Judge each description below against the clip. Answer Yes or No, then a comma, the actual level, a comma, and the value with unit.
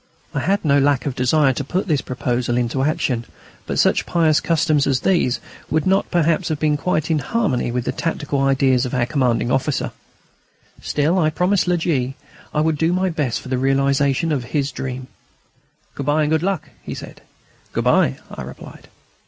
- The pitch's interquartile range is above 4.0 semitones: No, average, 3.7 semitones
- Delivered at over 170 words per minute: Yes, average, 190 wpm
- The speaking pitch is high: No, medium, 145 Hz